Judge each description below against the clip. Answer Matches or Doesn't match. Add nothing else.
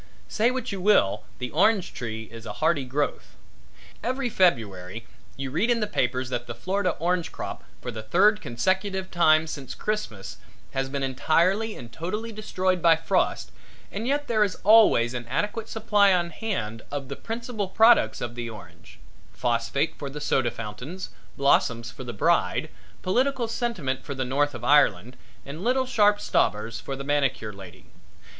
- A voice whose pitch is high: Doesn't match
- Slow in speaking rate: Doesn't match